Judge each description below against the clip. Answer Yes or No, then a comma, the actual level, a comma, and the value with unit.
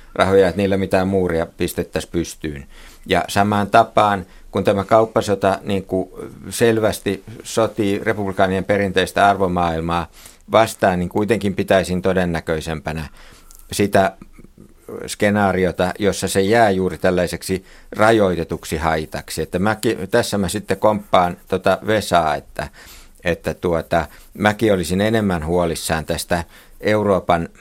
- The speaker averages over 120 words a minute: No, average, 110 wpm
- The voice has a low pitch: Yes, very low, 95 Hz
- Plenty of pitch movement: No, average, 2.8 semitones